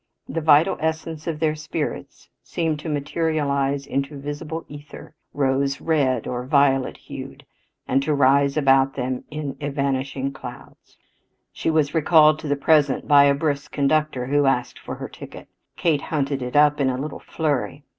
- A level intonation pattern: Yes, narrow, 2.0 semitones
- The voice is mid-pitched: Yes, medium, 145 Hz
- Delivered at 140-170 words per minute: Yes, average, 160 wpm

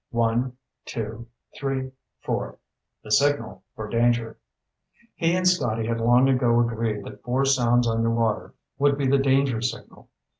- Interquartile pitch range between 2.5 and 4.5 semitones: Yes, average, 2.9 semitones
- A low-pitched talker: Yes, low, 120 Hz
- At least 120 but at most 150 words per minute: Yes, average, 140 wpm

